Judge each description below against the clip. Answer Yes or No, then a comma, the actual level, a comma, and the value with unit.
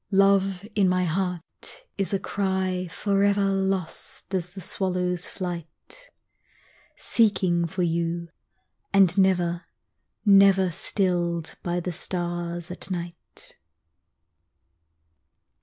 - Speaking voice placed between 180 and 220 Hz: Yes, medium, 185 Hz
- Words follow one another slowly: Yes, slow, 95 wpm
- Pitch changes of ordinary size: No, narrow, 2.1 semitones